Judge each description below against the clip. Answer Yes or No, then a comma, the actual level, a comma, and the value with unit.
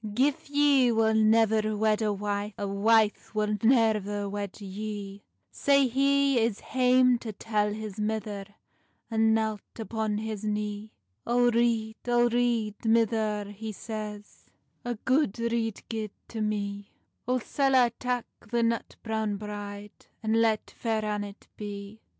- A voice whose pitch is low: No, high, 220 Hz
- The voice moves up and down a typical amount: No, narrow, 2.0 semitones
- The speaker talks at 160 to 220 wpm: No, average, 140 wpm